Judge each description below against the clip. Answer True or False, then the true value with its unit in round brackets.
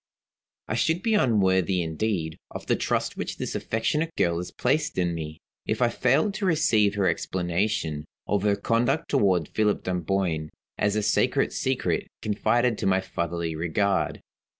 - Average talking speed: True (155 wpm)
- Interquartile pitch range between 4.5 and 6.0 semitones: True (4.9 semitones)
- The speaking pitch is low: True (100 Hz)